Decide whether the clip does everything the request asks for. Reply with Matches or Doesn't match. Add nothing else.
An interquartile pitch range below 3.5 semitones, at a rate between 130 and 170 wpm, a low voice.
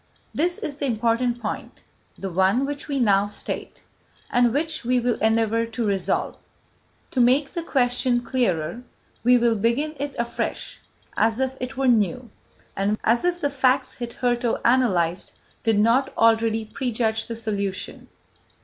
Doesn't match